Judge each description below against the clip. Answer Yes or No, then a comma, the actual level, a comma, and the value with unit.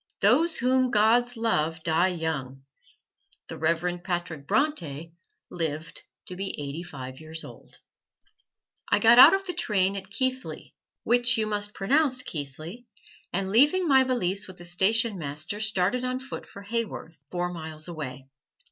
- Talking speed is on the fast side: No, average, 150 wpm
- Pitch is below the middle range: No, high, 190 Hz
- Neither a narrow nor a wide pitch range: No, wide, 7.1 semitones